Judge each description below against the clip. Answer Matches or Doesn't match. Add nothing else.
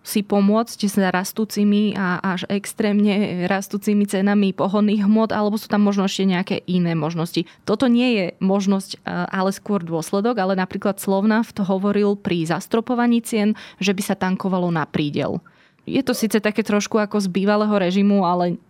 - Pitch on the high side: Matches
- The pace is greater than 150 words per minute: Matches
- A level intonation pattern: Matches